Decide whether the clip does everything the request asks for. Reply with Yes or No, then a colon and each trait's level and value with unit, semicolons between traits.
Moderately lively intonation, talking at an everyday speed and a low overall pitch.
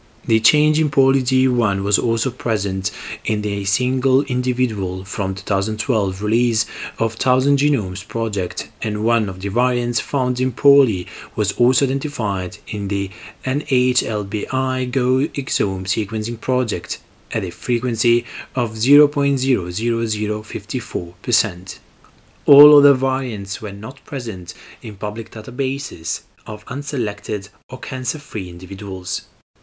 No: average, 4.1 semitones; slow, 115 wpm; low, 115 Hz